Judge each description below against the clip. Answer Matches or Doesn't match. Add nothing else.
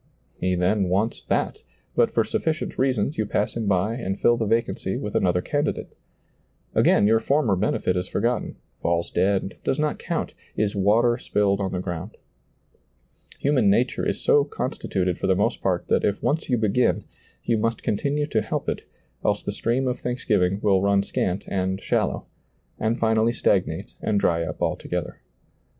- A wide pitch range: Doesn't match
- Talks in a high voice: Doesn't match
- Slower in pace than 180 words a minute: Matches